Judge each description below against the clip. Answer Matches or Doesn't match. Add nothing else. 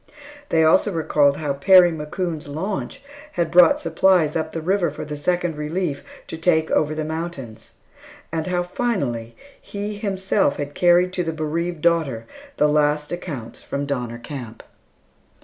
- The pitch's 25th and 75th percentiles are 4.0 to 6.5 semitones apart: Doesn't match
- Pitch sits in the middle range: Matches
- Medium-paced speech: Matches